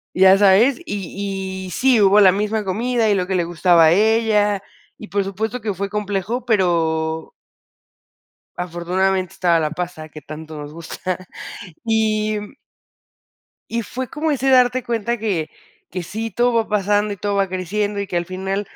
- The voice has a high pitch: Yes, high, 200 Hz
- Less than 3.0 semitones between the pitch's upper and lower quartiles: No, average, 3.3 semitones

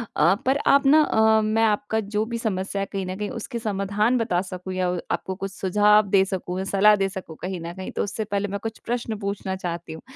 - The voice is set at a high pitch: Yes, high, 200 Hz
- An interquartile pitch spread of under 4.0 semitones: Yes, average, 2.7 semitones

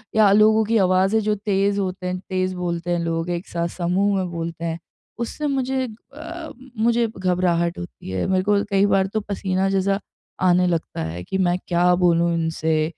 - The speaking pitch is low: No, medium, 185 Hz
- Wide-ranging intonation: No, average, 2.9 semitones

